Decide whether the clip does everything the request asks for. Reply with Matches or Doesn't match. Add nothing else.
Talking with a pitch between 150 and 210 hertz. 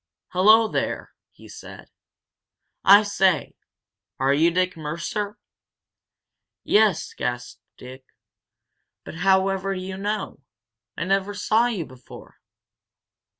Matches